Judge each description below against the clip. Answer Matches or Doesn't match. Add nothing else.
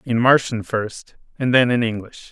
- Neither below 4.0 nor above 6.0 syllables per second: Matches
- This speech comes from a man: Matches